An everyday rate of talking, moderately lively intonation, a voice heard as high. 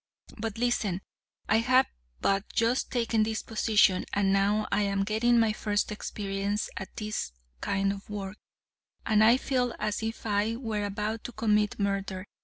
No: average, 160 wpm; narrow, 2.1 semitones; high, 210 Hz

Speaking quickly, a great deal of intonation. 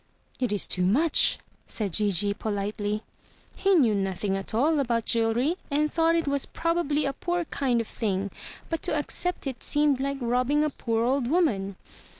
No: average, 170 wpm; wide, 6.3 semitones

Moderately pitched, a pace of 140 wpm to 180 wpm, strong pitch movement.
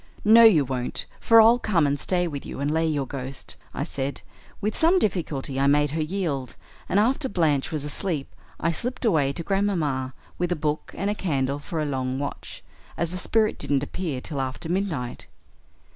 No: medium, 155 Hz; average, 190 wpm; wide, 5.8 semitones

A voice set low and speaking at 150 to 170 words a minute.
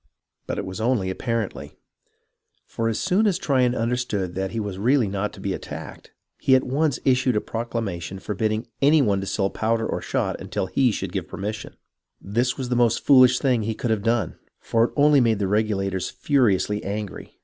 No: low, 115 Hz; average, 195 wpm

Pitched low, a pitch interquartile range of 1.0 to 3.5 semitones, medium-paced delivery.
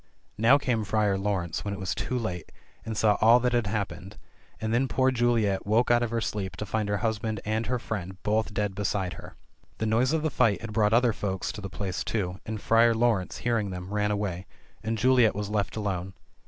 No: low, 105 Hz; average, 2.7 semitones; fast, 220 wpm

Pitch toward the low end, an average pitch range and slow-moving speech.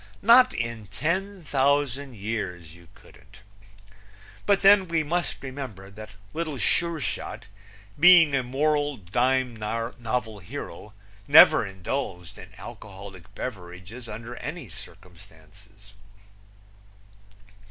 No: low, 115 Hz; wide, 6.7 semitones; slow, 100 wpm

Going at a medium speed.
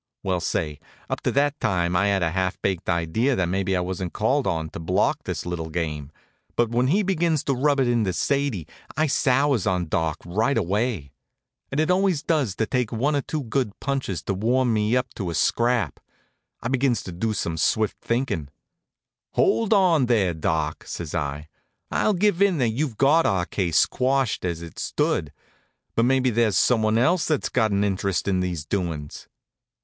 Yes: average, 185 wpm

